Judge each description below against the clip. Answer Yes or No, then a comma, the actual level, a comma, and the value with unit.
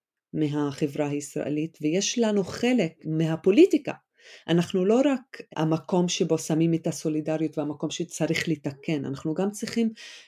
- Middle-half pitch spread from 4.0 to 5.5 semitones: Yes, average, 4.6 semitones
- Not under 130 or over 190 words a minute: No, average, 115 wpm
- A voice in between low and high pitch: Yes, medium, 165 Hz